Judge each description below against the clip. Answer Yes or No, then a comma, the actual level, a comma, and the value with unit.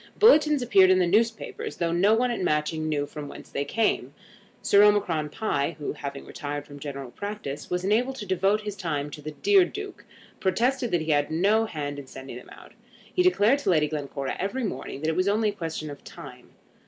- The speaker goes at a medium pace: No, fast, 210 wpm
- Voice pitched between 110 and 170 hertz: No, medium, 180 Hz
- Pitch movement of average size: No, wide, 6.7 semitones